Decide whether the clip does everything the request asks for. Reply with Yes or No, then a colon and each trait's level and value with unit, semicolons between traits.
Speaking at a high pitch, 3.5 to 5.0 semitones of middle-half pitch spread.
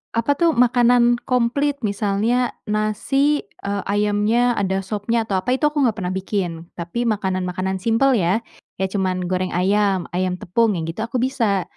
Yes: high, 210 Hz; average, 4.1 semitones